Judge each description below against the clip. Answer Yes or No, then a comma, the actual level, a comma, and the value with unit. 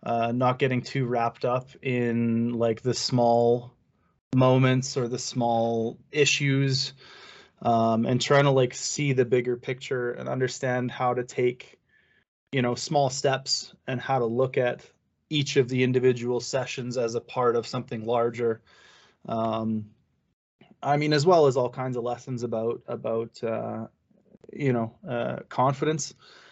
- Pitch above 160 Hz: No, low, 125 Hz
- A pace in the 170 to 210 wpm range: No, average, 150 wpm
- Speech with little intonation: Yes, narrow, 1.9 semitones